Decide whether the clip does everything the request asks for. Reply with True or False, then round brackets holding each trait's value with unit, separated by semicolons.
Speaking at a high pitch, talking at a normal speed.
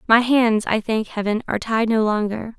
False (220 Hz; 210 wpm)